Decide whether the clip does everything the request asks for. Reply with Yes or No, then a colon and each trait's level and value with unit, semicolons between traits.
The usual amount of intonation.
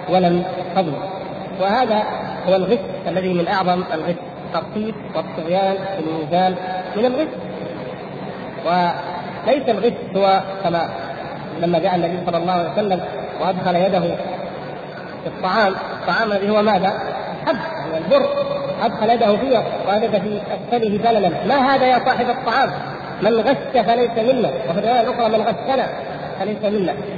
Yes: average, 4.1 semitones